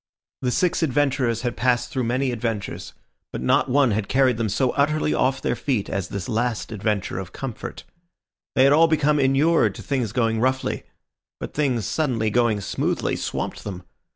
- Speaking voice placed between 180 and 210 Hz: No, low, 125 Hz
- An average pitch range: Yes, average, 3.6 semitones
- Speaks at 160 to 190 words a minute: Yes, average, 175 wpm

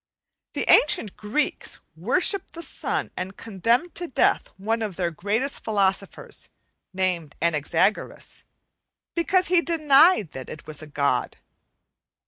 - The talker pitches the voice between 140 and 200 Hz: No, high, 210 Hz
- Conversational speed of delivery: No, slow, 120 wpm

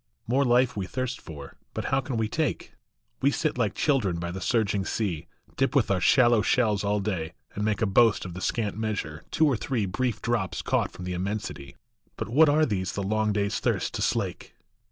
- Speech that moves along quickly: Yes, fast, 215 wpm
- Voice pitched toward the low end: Yes, low, 110 Hz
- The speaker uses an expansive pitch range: No, average, 4.7 semitones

